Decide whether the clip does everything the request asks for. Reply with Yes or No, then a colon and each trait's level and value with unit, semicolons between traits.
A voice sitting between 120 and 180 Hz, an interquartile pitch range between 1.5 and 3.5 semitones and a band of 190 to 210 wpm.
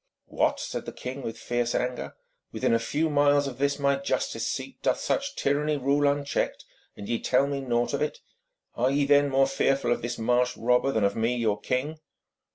Yes: low, 135 Hz; average, 2.8 semitones; average, 200 wpm